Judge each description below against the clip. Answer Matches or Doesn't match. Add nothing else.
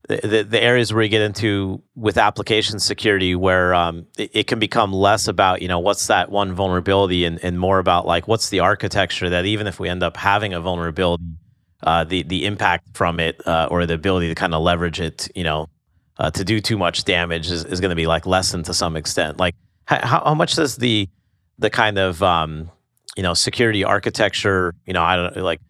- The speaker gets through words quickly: Matches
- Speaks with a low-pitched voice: Matches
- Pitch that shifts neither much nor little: Matches